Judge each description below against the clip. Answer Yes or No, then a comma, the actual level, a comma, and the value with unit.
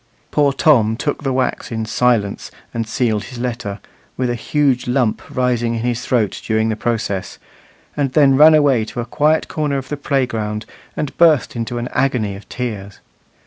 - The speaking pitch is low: Yes, low, 125 Hz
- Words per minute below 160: No, average, 180 wpm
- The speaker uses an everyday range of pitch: Yes, average, 3.6 semitones